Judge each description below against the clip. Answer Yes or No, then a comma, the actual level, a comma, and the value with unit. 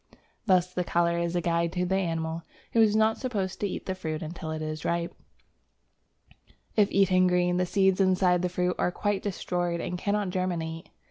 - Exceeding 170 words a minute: Yes, average, 190 wpm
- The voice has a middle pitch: Yes, medium, 180 Hz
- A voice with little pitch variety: Yes, narrow, 2.0 semitones